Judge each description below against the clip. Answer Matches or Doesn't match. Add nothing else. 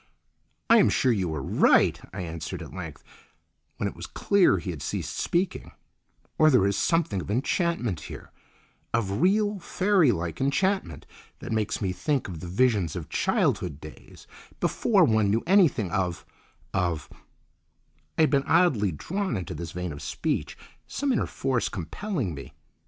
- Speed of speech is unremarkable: Matches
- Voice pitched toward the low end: Matches